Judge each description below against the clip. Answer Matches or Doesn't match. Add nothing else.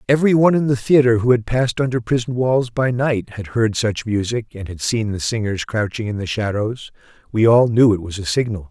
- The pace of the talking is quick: Matches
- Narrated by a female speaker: Doesn't match